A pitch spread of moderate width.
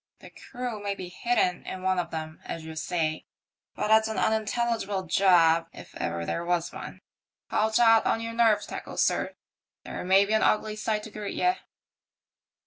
Yes: average, 4.0 semitones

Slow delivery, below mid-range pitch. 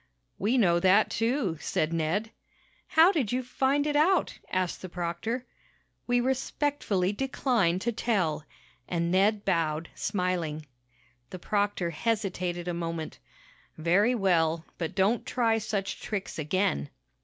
No: slow, 130 wpm; high, 195 Hz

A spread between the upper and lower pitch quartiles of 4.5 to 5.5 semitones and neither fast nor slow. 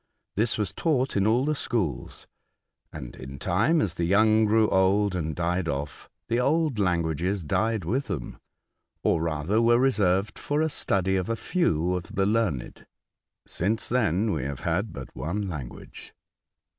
Yes: average, 5.1 semitones; average, 160 wpm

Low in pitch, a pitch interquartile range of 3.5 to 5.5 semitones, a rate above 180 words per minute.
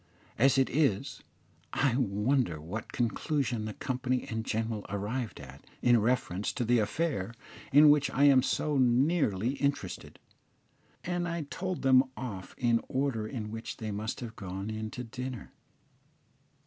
No: low, 120 Hz; average, 4.0 semitones; average, 150 wpm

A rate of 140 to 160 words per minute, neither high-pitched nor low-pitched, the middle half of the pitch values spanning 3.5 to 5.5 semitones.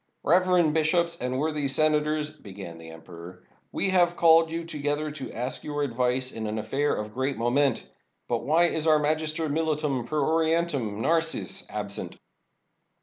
Yes: average, 150 wpm; medium, 150 Hz; average, 4.5 semitones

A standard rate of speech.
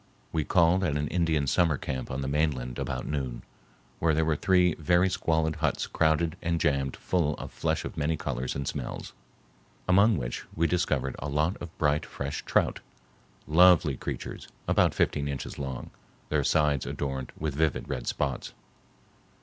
Yes: average, 165 wpm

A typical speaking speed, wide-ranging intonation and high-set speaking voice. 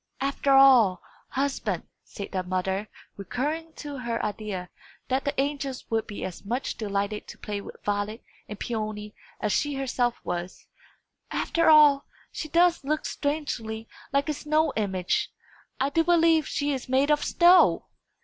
Yes: average, 150 wpm; wide, 5.8 semitones; very high, 260 Hz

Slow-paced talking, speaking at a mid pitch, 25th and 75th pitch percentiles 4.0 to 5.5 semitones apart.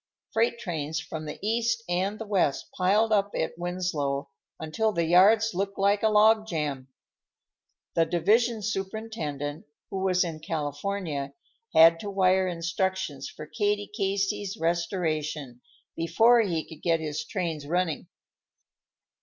Yes: slow, 130 wpm; medium, 180 Hz; average, 4.4 semitones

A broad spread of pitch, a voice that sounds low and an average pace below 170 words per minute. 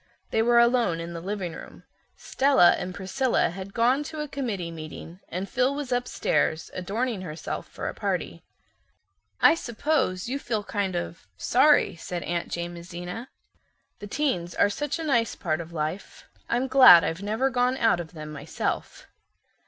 No: wide, 6.6 semitones; high, 200 Hz; average, 160 wpm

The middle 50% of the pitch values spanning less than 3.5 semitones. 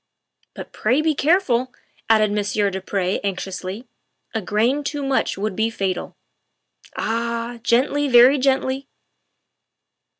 No: average, 4.5 semitones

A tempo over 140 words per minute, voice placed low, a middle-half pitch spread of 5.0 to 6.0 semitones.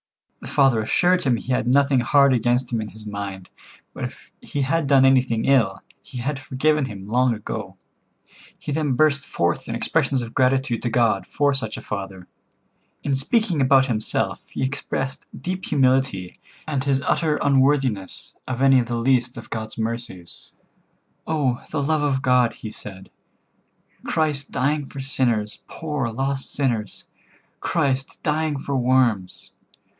No: average, 155 wpm; low, 130 Hz; average, 3.3 semitones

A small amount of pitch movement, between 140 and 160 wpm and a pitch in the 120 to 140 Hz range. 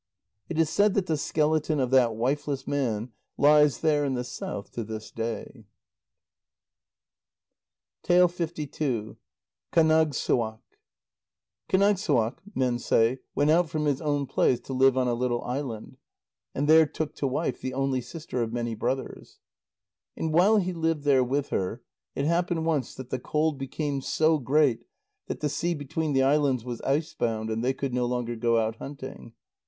No: average, 4.1 semitones; average, 155 wpm; low, 135 Hz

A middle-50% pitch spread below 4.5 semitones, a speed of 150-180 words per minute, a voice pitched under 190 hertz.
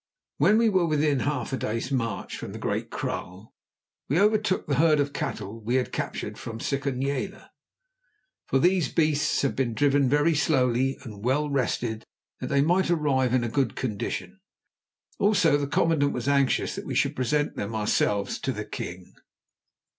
Yes: average, 4.1 semitones; average, 170 wpm; medium, 140 Hz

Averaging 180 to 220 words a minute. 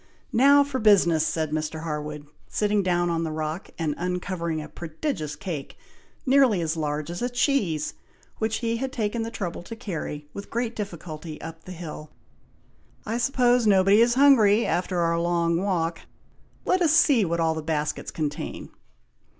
No: average, 165 wpm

